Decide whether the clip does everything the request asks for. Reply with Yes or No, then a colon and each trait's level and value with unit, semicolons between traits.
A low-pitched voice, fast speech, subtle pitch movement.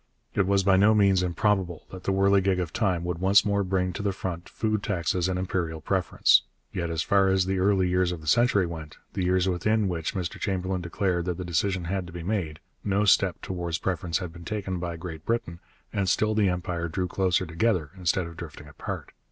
Yes: very low, 90 Hz; fast, 215 wpm; narrow, 2.3 semitones